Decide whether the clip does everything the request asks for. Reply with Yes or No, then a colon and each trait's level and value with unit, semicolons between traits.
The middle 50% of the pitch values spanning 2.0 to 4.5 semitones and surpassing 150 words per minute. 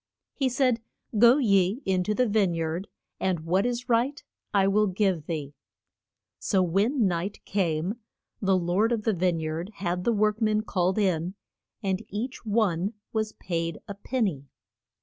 Yes: average, 3.8 semitones; average, 165 wpm